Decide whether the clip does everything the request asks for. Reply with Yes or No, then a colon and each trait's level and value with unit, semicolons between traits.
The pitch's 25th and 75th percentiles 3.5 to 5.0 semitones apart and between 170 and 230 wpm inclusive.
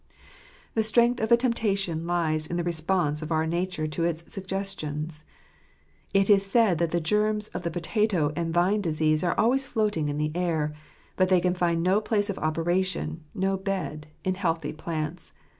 Yes: average, 3.8 semitones; average, 180 wpm